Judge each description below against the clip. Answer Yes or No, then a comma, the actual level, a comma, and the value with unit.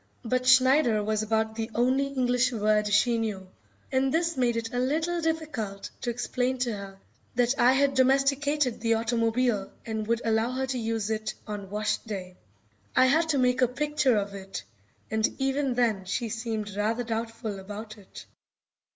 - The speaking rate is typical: Yes, average, 170 wpm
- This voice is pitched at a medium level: No, high, 235 Hz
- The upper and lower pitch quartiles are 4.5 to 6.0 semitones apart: No, average, 3.2 semitones